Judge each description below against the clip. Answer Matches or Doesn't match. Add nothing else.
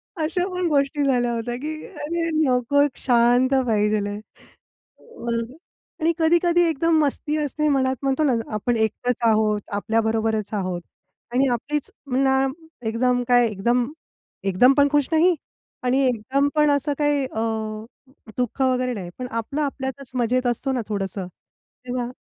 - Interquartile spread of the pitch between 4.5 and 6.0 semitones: Doesn't match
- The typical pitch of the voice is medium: Doesn't match